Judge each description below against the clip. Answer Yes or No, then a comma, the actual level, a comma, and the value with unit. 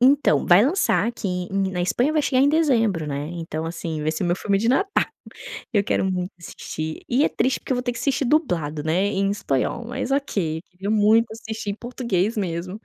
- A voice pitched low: No, high, 200 Hz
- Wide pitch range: Yes, wide, 6.1 semitones